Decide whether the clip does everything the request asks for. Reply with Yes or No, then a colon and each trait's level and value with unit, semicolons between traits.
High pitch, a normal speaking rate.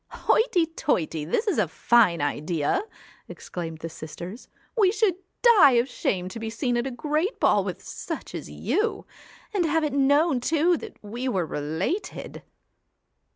Yes: very high, 255 Hz; average, 160 wpm